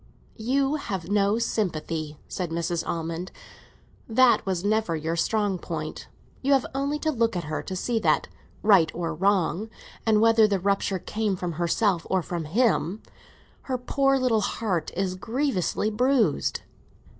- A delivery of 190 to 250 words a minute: No, average, 150 wpm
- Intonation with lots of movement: No, average, 5.0 semitones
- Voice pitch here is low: No, high, 200 Hz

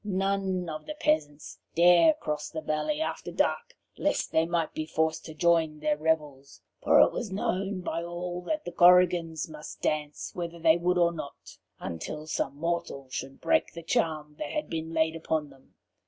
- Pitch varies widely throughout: No, average, 2.8 semitones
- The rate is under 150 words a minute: No, average, 180 wpm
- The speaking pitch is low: No, medium, 165 Hz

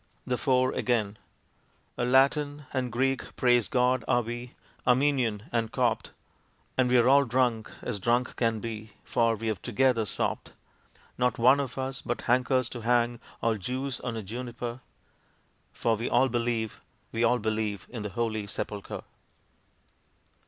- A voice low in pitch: Yes, low, 120 Hz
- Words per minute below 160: Yes, average, 145 wpm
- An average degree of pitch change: No, narrow, 2.2 semitones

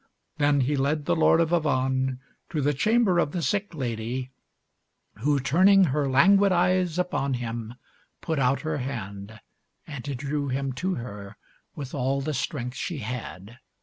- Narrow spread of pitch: No, average, 4.4 semitones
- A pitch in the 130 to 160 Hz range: Yes, medium, 140 Hz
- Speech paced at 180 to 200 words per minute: No, average, 155 wpm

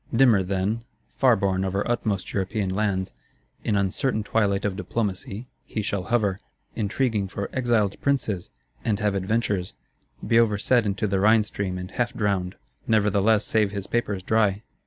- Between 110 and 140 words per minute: No, average, 150 wpm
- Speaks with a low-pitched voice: Yes, low, 105 Hz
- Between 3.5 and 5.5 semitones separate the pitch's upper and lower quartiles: No, narrow, 2.5 semitones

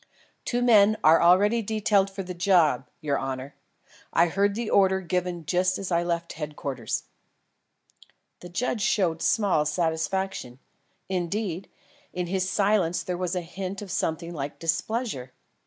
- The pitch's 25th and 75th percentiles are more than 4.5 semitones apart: No, average, 3.3 semitones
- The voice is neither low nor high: Yes, medium, 180 Hz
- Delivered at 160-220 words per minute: No, average, 140 wpm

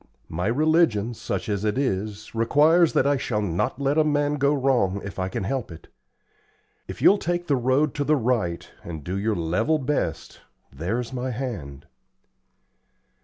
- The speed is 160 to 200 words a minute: Yes, average, 170 wpm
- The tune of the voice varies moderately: No, wide, 6.4 semitones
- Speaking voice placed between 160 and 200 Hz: No, low, 125 Hz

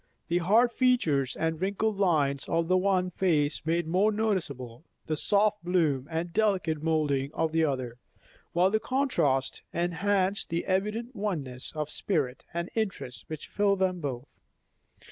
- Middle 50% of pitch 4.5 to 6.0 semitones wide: Yes, average, 5.1 semitones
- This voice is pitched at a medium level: Yes, medium, 170 Hz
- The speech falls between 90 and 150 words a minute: Yes, average, 145 wpm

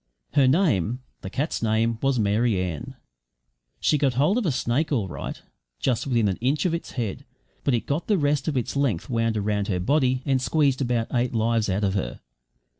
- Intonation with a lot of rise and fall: No, average, 4.5 semitones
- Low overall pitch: Yes, low, 125 Hz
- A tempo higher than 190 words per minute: Yes, average, 200 wpm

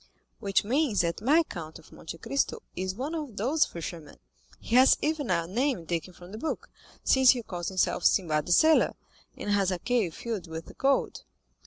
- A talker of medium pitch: No, high, 205 Hz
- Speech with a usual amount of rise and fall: No, wide, 7.3 semitones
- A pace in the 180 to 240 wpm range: Yes, average, 185 wpm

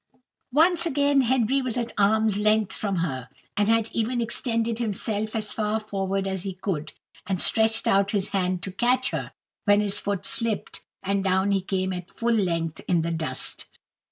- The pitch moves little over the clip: No, average, 3.2 semitones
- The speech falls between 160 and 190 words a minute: Yes, average, 180 wpm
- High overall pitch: Yes, high, 205 Hz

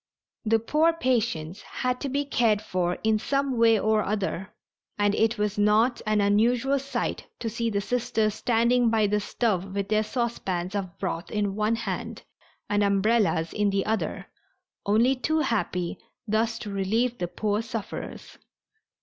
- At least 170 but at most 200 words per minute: No, average, 160 wpm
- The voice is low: No, high, 215 Hz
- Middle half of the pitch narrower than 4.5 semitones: Yes, average, 2.7 semitones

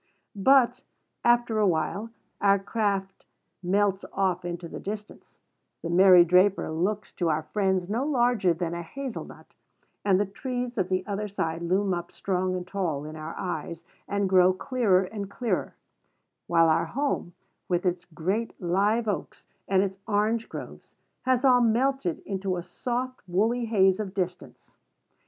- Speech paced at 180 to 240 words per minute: No, average, 155 wpm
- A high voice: Yes, high, 195 Hz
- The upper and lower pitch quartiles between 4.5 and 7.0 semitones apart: No, average, 3.7 semitones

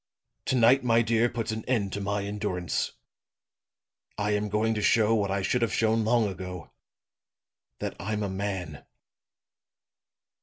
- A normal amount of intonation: No, narrow, 2.3 semitones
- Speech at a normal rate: Yes, average, 150 wpm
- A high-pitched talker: No, low, 105 Hz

